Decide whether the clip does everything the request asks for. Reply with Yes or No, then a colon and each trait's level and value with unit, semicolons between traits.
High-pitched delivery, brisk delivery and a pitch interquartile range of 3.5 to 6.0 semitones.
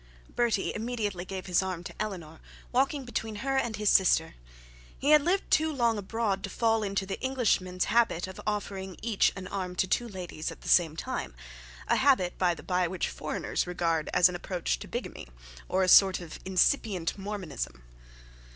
No: high, 195 Hz; average, 180 wpm; average, 4.0 semitones